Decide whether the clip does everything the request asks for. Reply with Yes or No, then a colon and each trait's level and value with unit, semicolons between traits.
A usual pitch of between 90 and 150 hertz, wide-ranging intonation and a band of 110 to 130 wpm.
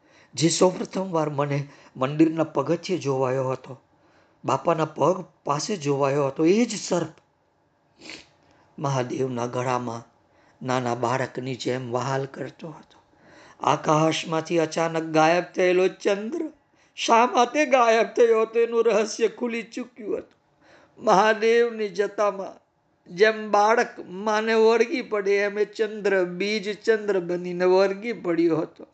No: medium, 180 Hz; wide, 7.0 semitones; average, 115 wpm